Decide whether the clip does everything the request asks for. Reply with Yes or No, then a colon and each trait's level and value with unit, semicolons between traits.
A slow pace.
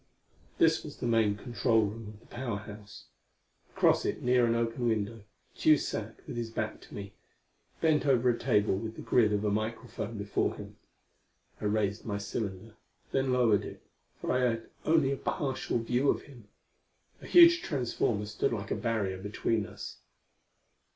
No: average, 170 wpm